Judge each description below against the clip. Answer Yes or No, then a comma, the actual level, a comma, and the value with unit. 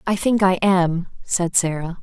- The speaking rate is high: No, average, 180 wpm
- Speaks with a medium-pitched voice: Yes, medium, 180 Hz